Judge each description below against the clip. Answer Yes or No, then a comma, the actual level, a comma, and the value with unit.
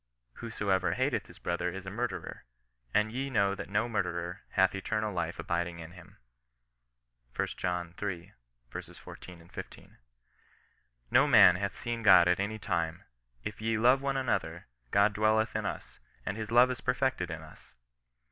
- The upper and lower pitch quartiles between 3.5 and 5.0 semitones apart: Yes, average, 4.1 semitones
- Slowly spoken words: No, average, 155 wpm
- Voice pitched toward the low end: Yes, low, 100 Hz